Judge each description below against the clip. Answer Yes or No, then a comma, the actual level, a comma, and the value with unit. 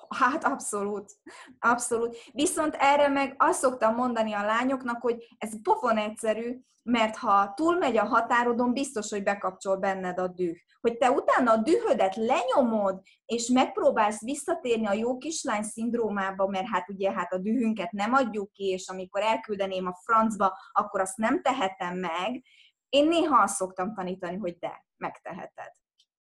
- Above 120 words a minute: Yes, average, 150 wpm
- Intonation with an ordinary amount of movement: Yes, average, 5.0 semitones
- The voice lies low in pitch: No, high, 225 Hz